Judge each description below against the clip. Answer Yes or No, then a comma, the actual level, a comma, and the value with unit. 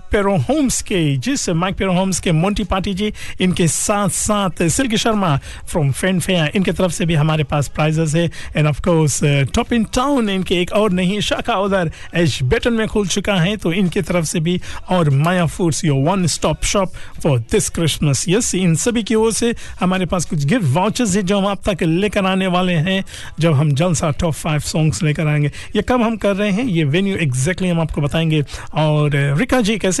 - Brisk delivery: Yes, fast, 210 wpm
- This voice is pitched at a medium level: Yes, medium, 180 Hz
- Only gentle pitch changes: No, average, 4.5 semitones